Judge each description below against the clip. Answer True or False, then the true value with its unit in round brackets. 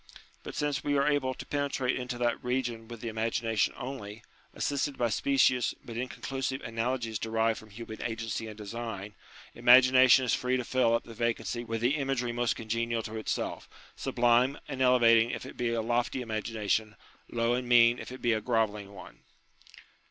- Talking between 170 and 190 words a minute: True (180 wpm)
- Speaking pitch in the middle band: False (120 Hz)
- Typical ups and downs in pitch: False (2.2 semitones)